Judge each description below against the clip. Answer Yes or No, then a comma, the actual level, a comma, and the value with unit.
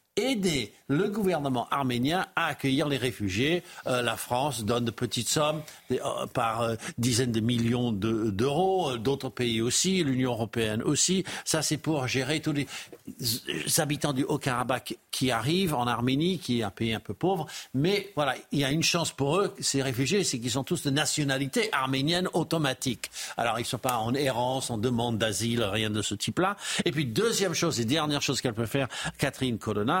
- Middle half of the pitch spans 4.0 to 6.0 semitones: Yes, average, 4.5 semitones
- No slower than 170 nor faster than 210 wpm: Yes, average, 190 wpm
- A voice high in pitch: No, low, 135 Hz